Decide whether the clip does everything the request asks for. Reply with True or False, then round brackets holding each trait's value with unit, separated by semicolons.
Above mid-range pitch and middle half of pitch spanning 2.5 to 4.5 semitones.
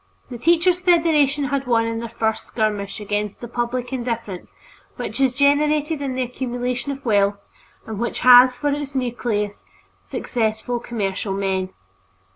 True (245 Hz; 4.2 semitones)